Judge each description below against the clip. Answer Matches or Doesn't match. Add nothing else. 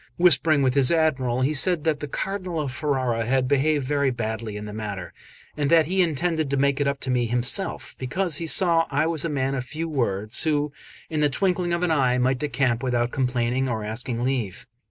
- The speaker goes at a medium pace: Doesn't match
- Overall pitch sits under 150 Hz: Matches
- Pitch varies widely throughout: Doesn't match